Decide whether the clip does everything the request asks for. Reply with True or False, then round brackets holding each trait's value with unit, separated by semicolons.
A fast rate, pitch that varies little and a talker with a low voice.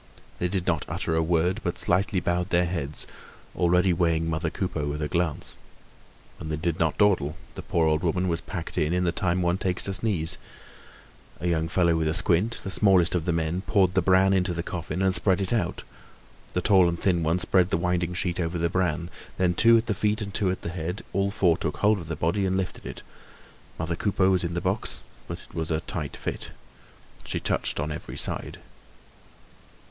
True (215 wpm; 2.3 semitones; 90 Hz)